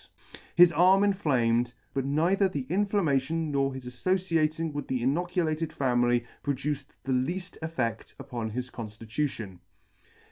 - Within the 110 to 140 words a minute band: Yes, slow, 135 wpm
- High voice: No, medium, 140 Hz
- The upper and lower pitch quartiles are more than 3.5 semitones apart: Yes, average, 5.2 semitones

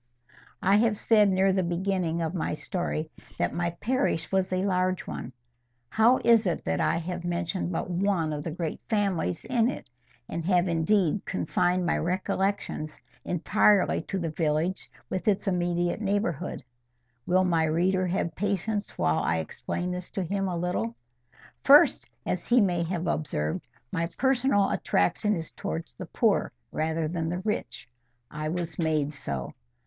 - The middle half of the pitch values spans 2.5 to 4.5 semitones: Yes, average, 3.2 semitones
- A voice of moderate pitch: Yes, medium, 180 Hz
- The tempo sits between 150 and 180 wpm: Yes, average, 160 wpm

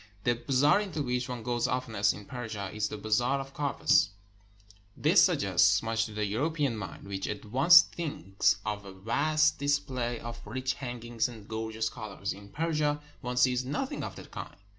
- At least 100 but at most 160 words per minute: No, average, 185 wpm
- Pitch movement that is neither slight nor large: Yes, average, 4.3 semitones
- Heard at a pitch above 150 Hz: No, low, 120 Hz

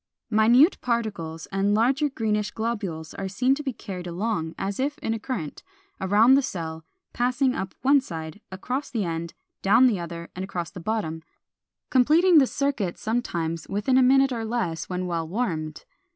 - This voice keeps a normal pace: Yes, average, 170 wpm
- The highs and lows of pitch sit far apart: Yes, wide, 6.7 semitones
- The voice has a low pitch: No, high, 210 Hz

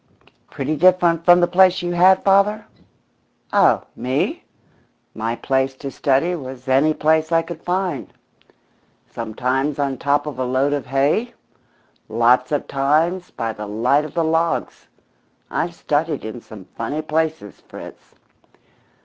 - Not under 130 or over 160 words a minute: Yes, average, 140 wpm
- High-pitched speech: No, medium, 150 Hz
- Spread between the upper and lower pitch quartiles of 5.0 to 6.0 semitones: No, average, 4.5 semitones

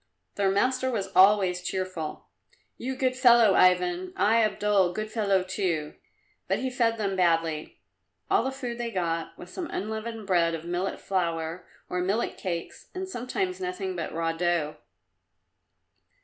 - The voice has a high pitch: Yes, high, 195 Hz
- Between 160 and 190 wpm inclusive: No, average, 150 wpm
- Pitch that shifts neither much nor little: Yes, average, 4.9 semitones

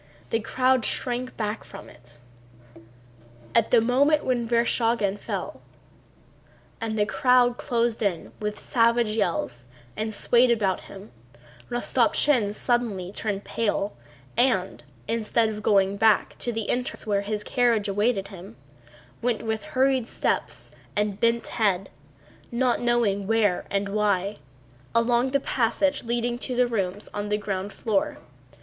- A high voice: Yes, high, 225 Hz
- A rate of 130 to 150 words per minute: Yes, slow, 135 wpm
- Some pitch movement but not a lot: Yes, average, 3.0 semitones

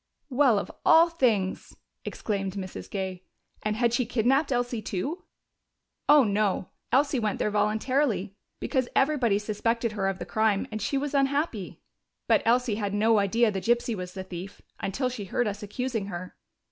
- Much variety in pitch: No, average, 4.2 semitones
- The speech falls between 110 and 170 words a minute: Yes, average, 165 wpm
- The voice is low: No, high, 220 Hz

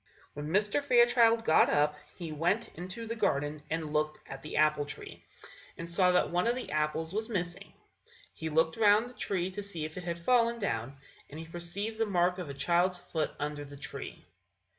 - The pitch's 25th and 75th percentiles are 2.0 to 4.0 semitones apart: No, average, 5.3 semitones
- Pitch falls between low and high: Yes, medium, 175 Hz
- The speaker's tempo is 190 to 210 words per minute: Yes, average, 200 wpm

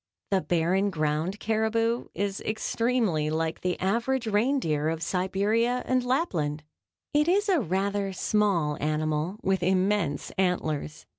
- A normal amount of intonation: No, wide, 5.9 semitones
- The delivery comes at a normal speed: No, slow, 125 wpm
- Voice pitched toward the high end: Yes, high, 195 Hz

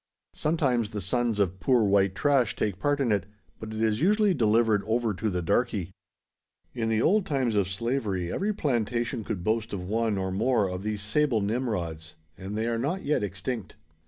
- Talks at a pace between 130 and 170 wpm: No, average, 190 wpm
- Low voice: Yes, low, 110 Hz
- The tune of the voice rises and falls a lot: No, average, 3.8 semitones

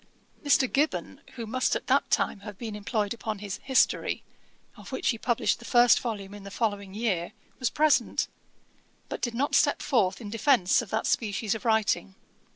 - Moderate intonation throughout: Yes, average, 3.0 semitones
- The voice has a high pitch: Yes, high, 220 Hz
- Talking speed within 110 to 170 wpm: No, average, 180 wpm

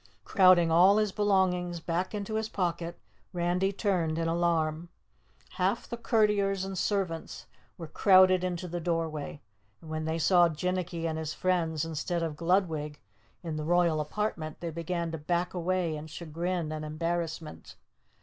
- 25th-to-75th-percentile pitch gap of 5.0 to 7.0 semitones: No, narrow, 2.5 semitones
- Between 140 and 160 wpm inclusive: Yes, average, 150 wpm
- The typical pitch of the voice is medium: Yes, medium, 170 Hz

